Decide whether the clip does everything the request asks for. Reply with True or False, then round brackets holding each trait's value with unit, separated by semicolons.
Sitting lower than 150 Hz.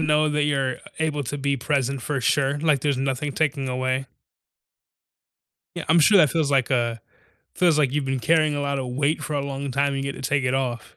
True (140 Hz)